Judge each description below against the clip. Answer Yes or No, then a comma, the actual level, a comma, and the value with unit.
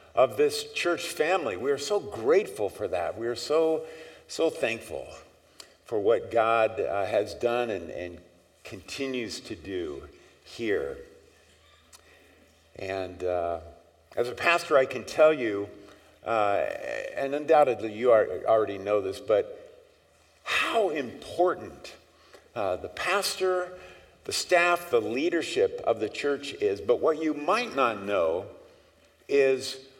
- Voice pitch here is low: No, medium, 160 Hz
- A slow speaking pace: Yes, slow, 130 wpm